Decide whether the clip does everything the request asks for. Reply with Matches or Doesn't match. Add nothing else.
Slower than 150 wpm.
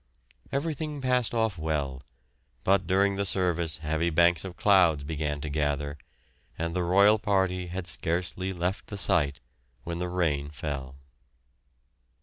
Matches